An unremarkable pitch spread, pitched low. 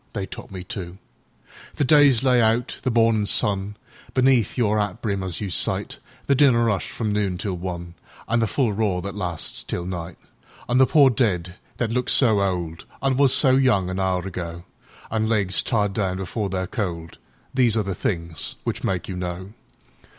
Yes: average, 4.4 semitones; low, 100 Hz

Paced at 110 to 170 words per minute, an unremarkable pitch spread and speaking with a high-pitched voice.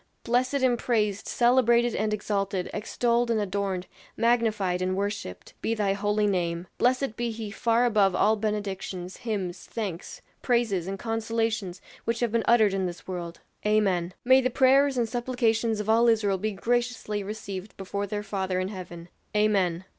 Yes: average, 160 wpm; average, 3.4 semitones; high, 210 Hz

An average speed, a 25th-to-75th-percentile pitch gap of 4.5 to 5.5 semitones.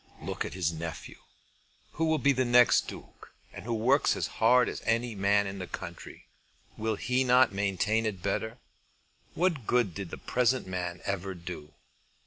Yes: average, 170 wpm; average, 4.8 semitones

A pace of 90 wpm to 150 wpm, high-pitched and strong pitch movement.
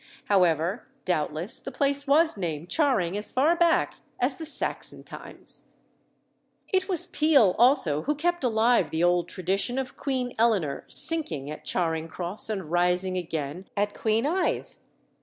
Yes: average, 140 wpm; high, 210 Hz; wide, 8.2 semitones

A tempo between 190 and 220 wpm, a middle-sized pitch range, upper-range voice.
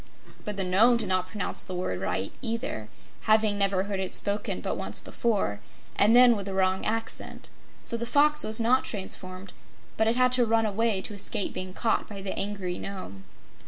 Yes: average, 195 wpm; average, 3.3 semitones; high, 205 Hz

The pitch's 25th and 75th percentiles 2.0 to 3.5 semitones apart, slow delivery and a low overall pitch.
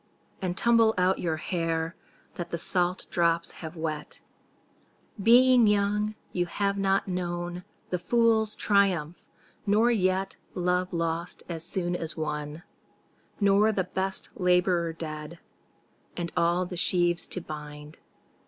No: average, 2.9 semitones; slow, 125 wpm; medium, 180 Hz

